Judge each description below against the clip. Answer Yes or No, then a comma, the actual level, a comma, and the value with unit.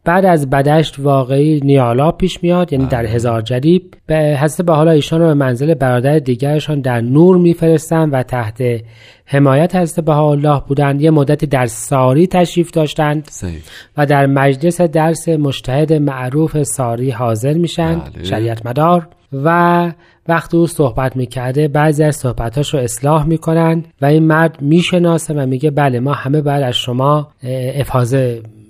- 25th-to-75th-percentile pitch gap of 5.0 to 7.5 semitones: No, average, 3.8 semitones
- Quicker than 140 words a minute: Yes, average, 150 wpm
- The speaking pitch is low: No, medium, 150 Hz